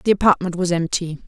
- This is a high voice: No, medium, 180 Hz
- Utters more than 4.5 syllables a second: Yes, 6.2 syllables/s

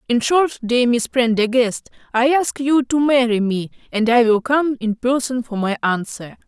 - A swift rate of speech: No, average, 185 wpm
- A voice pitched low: No, high, 245 Hz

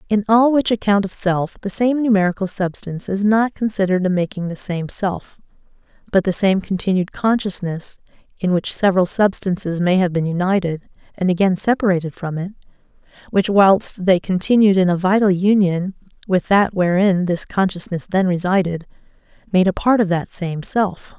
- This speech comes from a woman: Yes, female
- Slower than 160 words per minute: No, average, 165 wpm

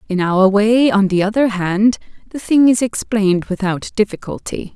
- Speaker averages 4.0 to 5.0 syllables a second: Yes, 4.8 syllables/s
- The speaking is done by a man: No, female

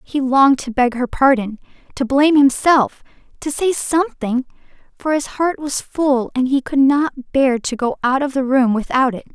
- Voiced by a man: No, female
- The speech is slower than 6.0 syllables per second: Yes, 4.7 syllables/s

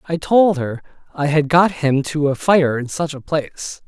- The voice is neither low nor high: Yes, medium, 150 Hz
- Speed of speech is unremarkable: No, fast, 215 wpm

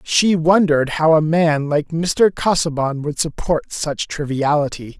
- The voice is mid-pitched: Yes, medium, 155 Hz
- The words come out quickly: No, average, 145 wpm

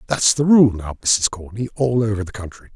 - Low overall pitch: Yes, low, 110 Hz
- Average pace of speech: No, fast, 220 wpm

